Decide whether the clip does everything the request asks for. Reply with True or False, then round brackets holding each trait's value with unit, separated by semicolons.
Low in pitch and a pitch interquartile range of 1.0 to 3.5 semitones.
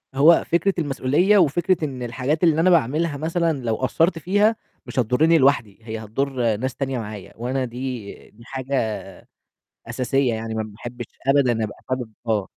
False (130 Hz; 5.4 semitones)